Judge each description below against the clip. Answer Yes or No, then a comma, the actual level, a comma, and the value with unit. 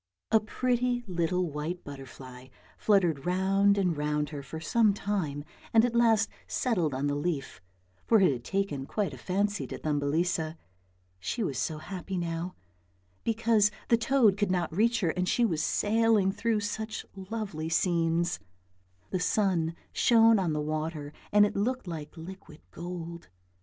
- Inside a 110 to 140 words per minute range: No, average, 155 wpm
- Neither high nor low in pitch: Yes, medium, 180 Hz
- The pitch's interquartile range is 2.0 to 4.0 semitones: No, average, 5.0 semitones